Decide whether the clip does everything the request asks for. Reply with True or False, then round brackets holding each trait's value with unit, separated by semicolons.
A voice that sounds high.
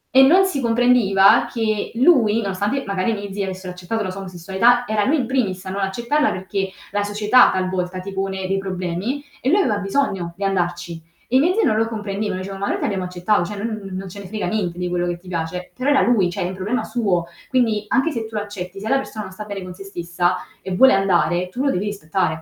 True (195 Hz)